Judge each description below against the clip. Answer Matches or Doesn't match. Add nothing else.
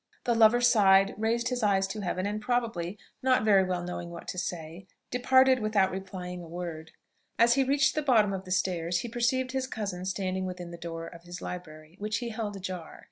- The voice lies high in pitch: Matches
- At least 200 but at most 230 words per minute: Matches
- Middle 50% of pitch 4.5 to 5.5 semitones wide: Matches